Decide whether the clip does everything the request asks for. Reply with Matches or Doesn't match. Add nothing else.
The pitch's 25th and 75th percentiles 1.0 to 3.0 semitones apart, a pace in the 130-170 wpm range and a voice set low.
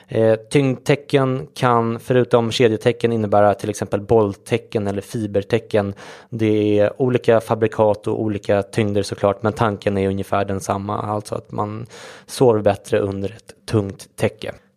Matches